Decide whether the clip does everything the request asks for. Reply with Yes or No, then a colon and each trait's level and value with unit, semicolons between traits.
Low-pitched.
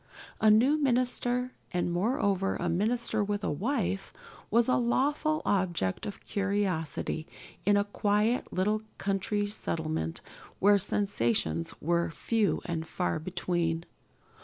No: high, 200 Hz